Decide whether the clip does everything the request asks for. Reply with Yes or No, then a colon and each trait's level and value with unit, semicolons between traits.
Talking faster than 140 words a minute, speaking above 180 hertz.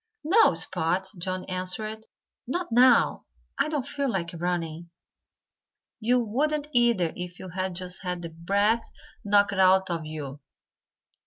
No: slow, 135 wpm; high, 190 Hz